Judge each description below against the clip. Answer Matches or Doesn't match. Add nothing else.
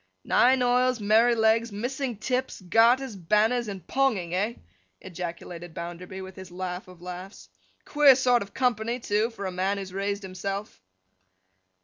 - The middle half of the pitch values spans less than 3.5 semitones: Doesn't match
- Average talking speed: Matches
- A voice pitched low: Doesn't match